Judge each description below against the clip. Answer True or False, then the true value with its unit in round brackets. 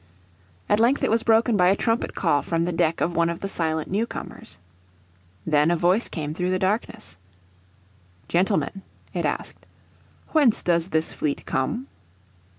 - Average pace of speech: True (160 wpm)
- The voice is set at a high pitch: False (180 Hz)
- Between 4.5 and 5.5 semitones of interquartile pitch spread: True (4.8 semitones)